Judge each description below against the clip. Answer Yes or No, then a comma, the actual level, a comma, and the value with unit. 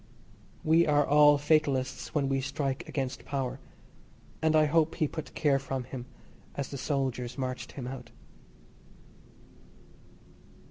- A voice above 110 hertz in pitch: Yes, medium, 140 Hz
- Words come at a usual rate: No, slow, 130 wpm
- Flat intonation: Yes, narrow, 2.3 semitones